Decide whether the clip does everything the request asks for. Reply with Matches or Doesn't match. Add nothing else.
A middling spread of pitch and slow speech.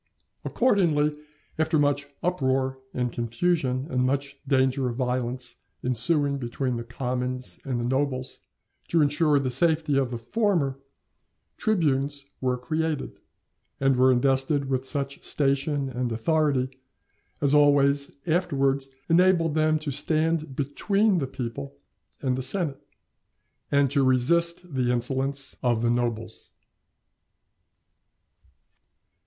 Matches